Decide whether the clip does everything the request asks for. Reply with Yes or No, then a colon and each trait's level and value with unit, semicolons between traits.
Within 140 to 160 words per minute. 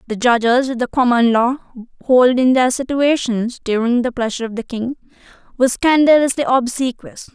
Yes: average, 145 wpm